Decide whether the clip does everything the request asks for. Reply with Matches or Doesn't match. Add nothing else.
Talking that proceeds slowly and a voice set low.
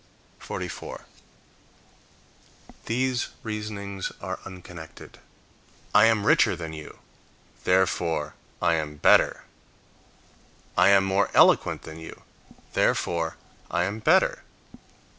Matches